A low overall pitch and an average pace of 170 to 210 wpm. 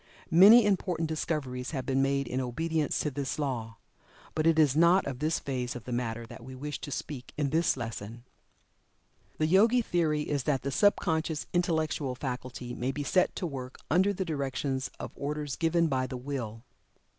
No: medium, 145 Hz; average, 185 wpm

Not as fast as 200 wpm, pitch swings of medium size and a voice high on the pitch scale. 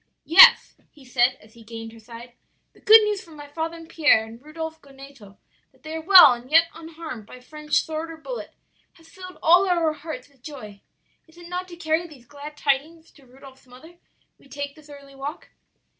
No: fast, 205 wpm; average, 4.1 semitones; very high, 300 Hz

